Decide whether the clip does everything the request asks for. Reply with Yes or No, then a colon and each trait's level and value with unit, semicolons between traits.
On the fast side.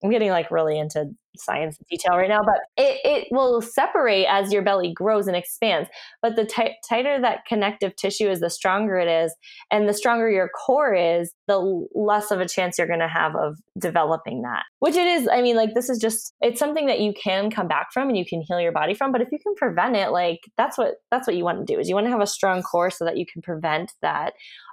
Yes: fast, 255 wpm